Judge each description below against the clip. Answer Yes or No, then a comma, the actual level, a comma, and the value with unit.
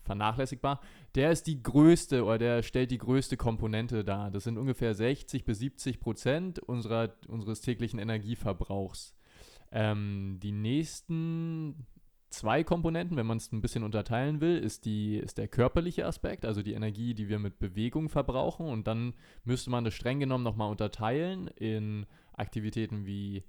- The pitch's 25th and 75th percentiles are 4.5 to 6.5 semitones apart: No, average, 3.8 semitones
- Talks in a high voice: No, low, 115 Hz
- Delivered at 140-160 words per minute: Yes, average, 155 wpm